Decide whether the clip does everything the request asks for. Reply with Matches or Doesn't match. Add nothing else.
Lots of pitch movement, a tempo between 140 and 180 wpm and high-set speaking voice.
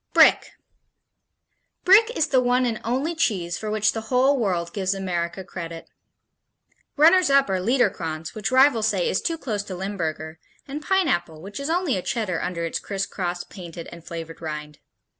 Matches